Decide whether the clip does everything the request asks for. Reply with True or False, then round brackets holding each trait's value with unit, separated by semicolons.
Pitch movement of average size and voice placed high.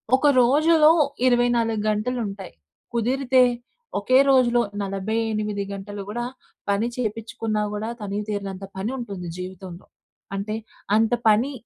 True (3.2 semitones; 215 Hz)